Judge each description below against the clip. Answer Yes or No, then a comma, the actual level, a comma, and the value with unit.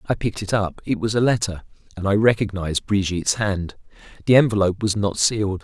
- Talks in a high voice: No, low, 100 Hz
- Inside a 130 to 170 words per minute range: No, average, 190 wpm